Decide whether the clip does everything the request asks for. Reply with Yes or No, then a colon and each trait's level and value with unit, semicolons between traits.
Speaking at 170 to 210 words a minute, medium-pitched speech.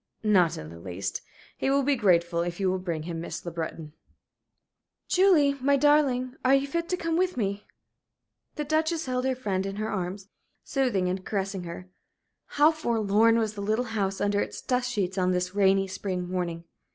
No: average, 190 wpm; high, 205 Hz